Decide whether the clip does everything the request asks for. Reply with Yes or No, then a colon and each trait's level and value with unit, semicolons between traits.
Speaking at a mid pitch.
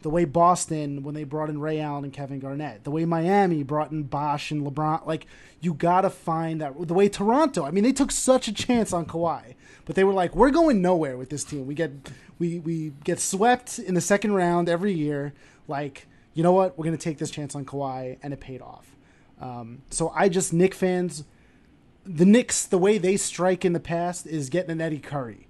Yes: medium, 165 Hz